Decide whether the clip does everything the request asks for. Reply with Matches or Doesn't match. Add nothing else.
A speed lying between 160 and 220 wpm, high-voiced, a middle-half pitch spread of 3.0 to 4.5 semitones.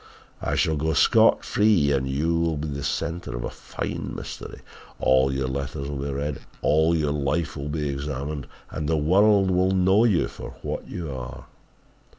Doesn't match